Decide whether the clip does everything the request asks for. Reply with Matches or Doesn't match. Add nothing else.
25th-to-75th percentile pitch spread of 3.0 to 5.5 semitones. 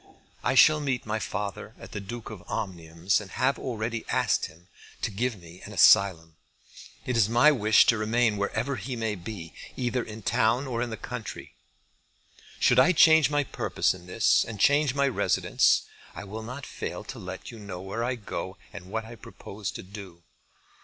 Matches